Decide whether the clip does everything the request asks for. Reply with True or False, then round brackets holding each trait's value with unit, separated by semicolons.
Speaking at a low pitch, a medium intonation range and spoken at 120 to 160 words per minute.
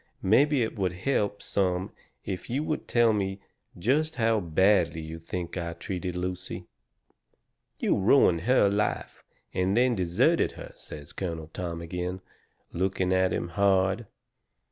True (95 Hz; 3.3 semitones; 140 wpm)